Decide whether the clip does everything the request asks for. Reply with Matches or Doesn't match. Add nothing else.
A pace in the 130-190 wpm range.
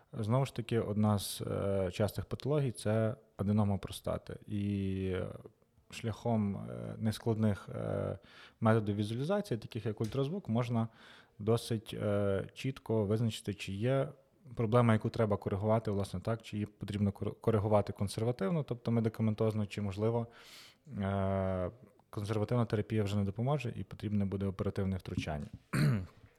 Doesn't match